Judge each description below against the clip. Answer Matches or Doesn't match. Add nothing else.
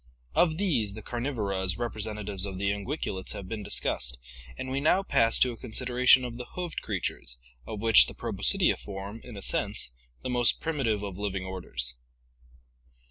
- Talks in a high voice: Doesn't match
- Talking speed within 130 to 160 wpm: Doesn't match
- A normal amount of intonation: Matches